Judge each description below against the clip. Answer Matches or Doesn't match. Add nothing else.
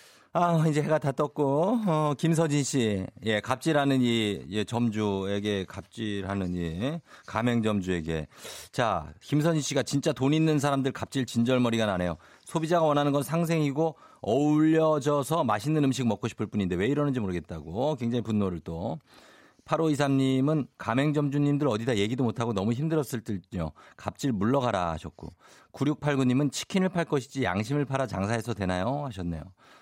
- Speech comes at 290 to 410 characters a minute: Matches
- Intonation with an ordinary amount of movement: Doesn't match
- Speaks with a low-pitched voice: Matches